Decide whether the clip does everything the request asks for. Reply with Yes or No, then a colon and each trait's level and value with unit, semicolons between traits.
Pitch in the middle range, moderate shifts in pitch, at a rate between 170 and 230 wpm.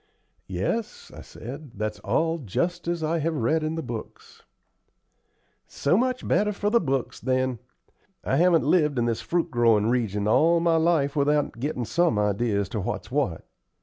No: medium, 145 Hz; wide, 6.2 semitones; average, 175 wpm